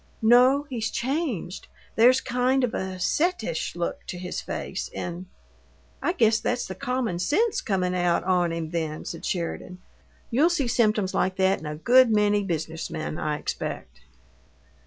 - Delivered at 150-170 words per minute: Yes, average, 160 wpm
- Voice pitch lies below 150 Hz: No, high, 200 Hz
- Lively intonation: Yes, wide, 6.1 semitones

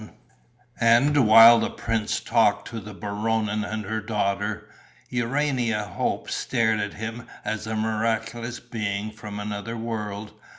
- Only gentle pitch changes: Yes, narrow, 1.7 semitones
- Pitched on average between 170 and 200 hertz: No, low, 110 Hz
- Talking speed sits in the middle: No, slow, 130 wpm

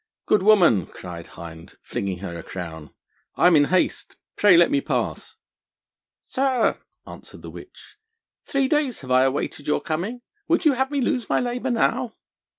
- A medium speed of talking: Yes, average, 165 wpm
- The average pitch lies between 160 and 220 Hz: Yes, medium, 185 Hz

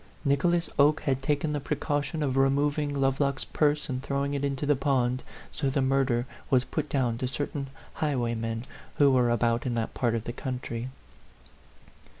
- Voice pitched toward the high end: No, low, 135 Hz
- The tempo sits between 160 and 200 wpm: Yes, average, 170 wpm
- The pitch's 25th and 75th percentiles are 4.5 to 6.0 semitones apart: No, narrow, 2.5 semitones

